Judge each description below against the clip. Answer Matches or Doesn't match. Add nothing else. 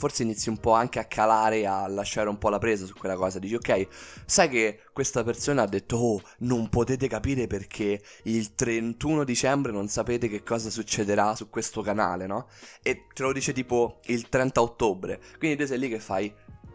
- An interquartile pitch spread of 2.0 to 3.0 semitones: Matches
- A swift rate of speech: Matches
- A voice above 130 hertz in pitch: Doesn't match